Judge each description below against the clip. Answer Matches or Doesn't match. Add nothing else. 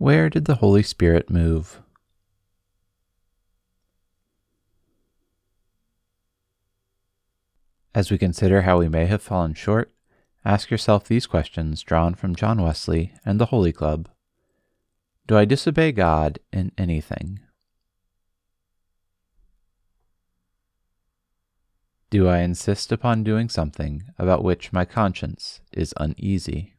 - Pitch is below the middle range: Matches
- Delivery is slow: Matches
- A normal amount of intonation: Doesn't match